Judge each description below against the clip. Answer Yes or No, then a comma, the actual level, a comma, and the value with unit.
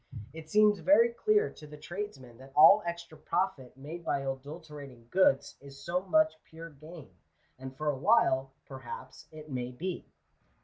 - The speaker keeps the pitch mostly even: No, wide, 5.4 semitones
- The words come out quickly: No, average, 160 wpm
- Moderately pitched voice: Yes, medium, 155 Hz